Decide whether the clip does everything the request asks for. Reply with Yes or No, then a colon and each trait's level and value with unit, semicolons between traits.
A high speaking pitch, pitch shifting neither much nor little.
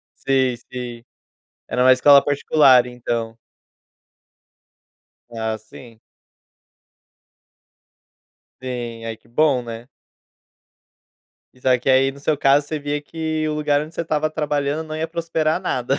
No: low, 135 Hz; average, 3.7 semitones